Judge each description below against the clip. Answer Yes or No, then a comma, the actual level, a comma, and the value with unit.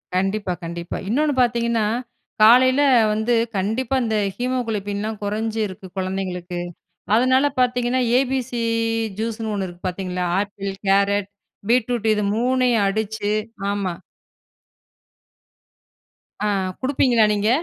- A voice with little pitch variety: No, average, 3.7 semitones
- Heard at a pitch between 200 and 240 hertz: Yes, high, 220 Hz